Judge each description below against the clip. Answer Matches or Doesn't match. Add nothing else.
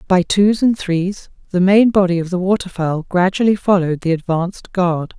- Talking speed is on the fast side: Doesn't match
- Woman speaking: Matches